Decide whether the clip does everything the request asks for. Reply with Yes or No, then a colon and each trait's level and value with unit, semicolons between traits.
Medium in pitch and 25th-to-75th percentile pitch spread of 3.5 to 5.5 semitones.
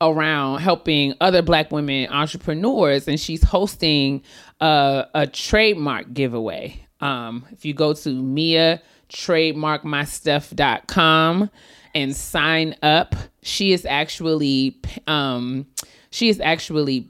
No: medium, 150 Hz; average, 2.7 semitones